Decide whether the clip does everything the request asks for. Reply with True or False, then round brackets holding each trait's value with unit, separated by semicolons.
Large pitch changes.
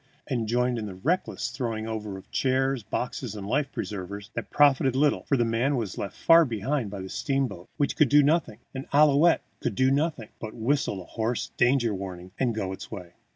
False (4.7 semitones)